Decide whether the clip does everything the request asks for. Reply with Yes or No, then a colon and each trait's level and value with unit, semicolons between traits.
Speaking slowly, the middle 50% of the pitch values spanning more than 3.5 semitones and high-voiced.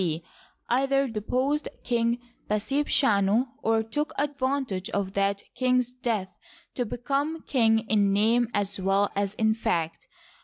Yes: slow, 125 wpm; average, 4.4 semitones; high, 225 Hz